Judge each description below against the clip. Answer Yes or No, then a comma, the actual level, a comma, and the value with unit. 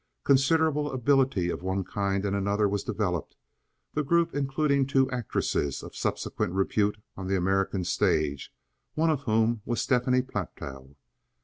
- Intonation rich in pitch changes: Yes, wide, 6.0 semitones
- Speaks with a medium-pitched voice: No, low, 110 Hz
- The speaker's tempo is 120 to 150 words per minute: Yes, average, 140 wpm